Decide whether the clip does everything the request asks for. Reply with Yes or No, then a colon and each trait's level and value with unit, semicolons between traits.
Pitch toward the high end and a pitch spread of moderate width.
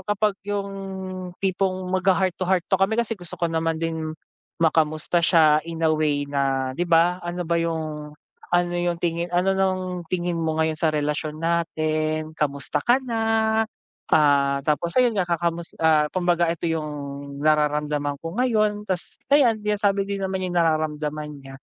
No: medium, 170 Hz; average, 3.2 semitones